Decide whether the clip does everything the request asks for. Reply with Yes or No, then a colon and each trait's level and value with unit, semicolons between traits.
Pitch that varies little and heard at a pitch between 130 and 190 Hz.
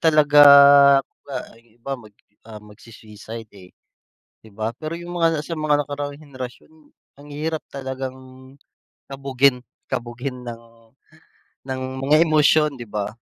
No: average, 4.3 semitones; low, 135 Hz